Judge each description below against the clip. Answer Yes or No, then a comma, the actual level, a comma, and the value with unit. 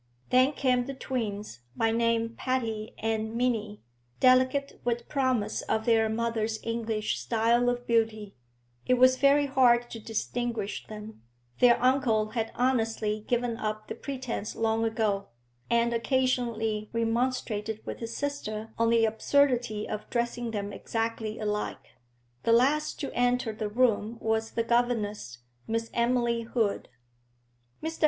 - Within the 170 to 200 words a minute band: No, slow, 135 wpm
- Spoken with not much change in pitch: Yes, narrow, 2.1 semitones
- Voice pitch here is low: No, high, 230 Hz